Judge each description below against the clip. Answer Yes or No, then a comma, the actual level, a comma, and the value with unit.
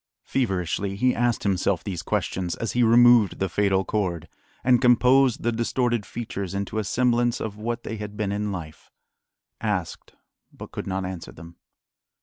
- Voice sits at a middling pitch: No, low, 105 Hz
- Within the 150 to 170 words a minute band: Yes, average, 160 wpm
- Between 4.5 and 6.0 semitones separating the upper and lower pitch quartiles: No, average, 3.8 semitones